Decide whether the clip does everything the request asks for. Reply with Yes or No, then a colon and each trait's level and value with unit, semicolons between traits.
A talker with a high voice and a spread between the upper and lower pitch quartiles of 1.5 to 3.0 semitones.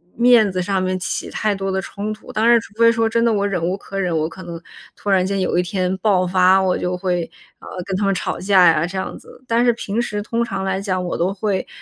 Yes: high, 195 Hz; narrow, 2.6 semitones